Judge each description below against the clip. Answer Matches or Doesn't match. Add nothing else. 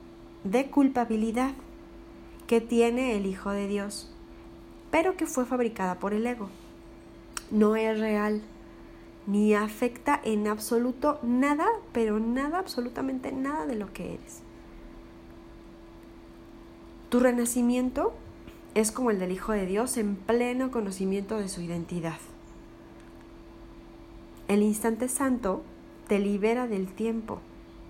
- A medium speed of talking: Doesn't match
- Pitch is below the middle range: Doesn't match